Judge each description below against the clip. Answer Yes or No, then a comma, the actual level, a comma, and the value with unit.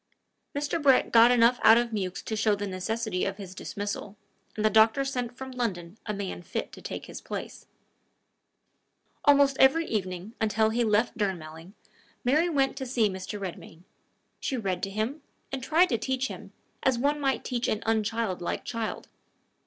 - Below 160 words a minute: No, average, 170 wpm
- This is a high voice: Yes, high, 225 Hz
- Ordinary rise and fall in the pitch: Yes, average, 4.7 semitones